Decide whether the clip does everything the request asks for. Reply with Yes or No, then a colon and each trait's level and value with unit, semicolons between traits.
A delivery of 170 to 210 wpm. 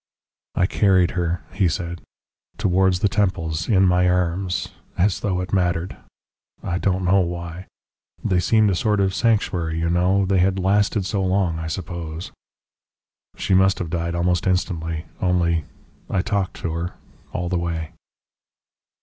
No: average, 150 wpm